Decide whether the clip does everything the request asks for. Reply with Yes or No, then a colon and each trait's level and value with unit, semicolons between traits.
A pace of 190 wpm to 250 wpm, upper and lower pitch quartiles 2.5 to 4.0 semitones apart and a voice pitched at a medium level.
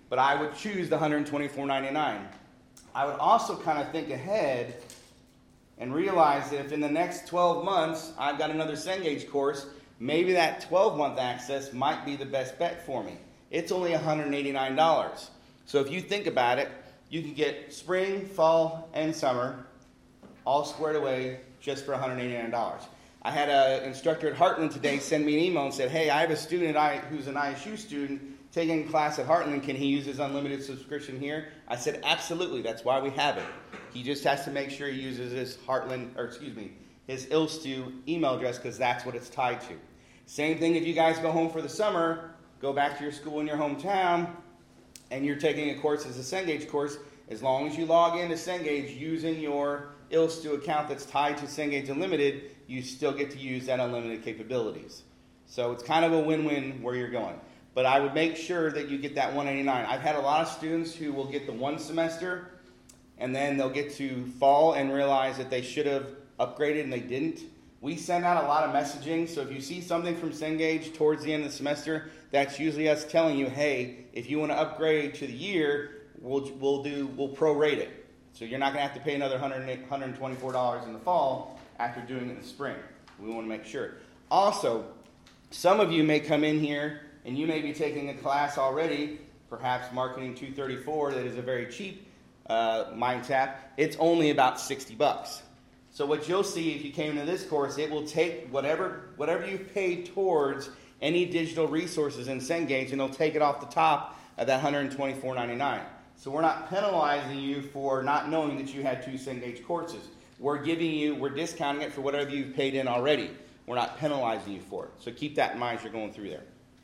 Yes: fast, 205 wpm; average, 2.8 semitones; medium, 145 Hz